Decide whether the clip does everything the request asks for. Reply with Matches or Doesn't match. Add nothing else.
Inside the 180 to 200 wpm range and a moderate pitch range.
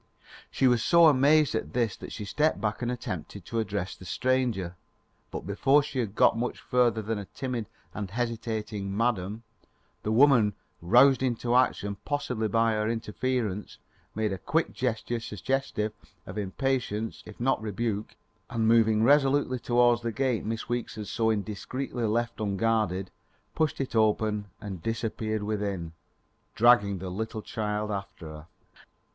Doesn't match